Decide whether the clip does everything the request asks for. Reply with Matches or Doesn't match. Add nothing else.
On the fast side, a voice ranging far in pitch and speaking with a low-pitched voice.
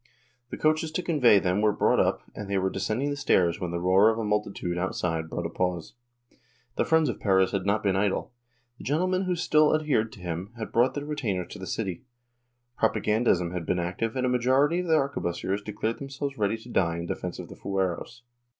Matches